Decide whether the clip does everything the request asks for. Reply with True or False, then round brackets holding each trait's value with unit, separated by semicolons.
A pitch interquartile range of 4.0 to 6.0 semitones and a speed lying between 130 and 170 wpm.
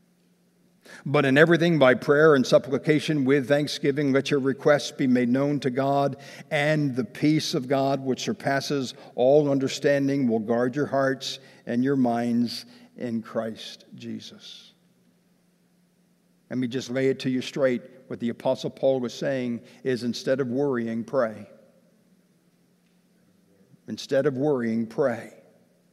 True (4.3 semitones; 135 wpm)